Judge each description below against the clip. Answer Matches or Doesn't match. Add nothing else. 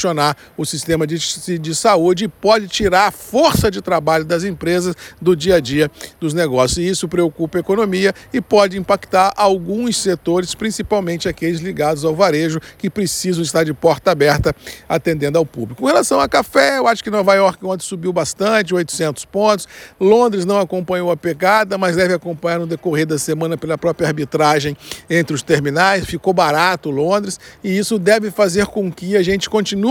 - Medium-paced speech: Matches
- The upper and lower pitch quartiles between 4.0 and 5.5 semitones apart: Doesn't match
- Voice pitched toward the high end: Doesn't match